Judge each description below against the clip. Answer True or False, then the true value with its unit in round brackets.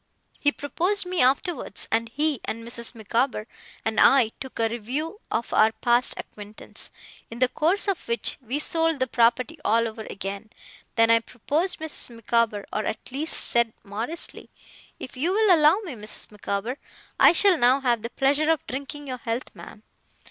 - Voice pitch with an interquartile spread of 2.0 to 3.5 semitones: False (4.9 semitones)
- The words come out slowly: False (170 wpm)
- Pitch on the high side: True (250 Hz)